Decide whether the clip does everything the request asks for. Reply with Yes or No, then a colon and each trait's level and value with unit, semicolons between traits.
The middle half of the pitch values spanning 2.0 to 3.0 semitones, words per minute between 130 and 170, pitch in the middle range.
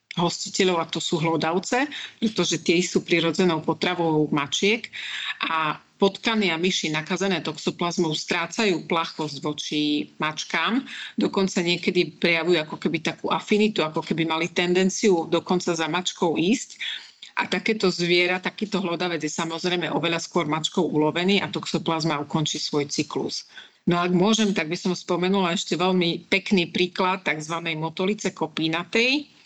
Yes: average, 2.7 semitones; average, 135 wpm; medium, 175 Hz